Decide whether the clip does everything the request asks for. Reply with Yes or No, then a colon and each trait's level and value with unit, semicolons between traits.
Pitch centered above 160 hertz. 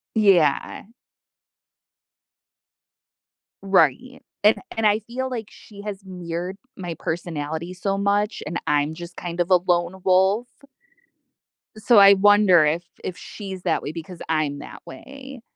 Yes: medium, 185 Hz